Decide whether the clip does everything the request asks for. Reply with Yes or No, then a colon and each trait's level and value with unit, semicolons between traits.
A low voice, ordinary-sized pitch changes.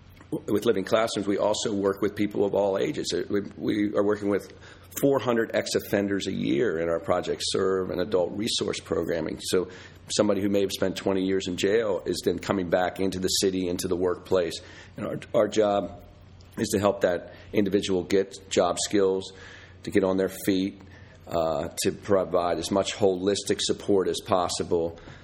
No: very low, 95 Hz; narrow, 1.5 semitones